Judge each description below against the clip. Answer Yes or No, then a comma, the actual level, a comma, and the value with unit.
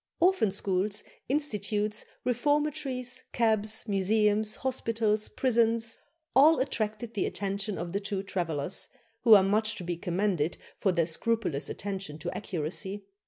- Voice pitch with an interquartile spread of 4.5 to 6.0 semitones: No, average, 3.2 semitones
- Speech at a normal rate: No, slow, 125 wpm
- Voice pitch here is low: No, high, 210 Hz